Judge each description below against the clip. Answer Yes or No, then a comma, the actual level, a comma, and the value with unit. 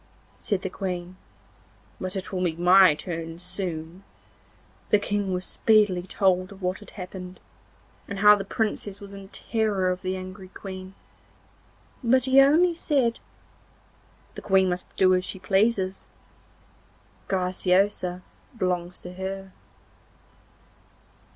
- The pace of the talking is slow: Yes, slow, 125 wpm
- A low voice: No, high, 190 Hz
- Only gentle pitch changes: Yes, narrow, 1.9 semitones